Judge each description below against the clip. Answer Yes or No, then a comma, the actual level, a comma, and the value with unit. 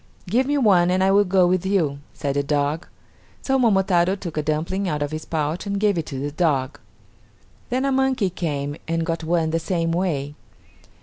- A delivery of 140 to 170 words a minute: No, average, 200 wpm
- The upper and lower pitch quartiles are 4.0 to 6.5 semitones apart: Yes, average, 4.3 semitones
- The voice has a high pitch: No, medium, 170 Hz